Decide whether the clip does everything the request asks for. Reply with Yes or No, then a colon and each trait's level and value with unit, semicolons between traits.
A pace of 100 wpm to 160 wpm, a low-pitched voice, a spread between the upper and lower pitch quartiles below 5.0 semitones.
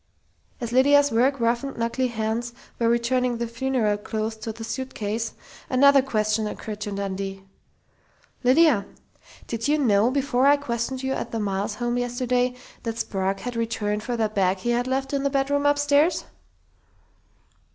No: average, 155 wpm; high, 235 Hz; average, 3.5 semitones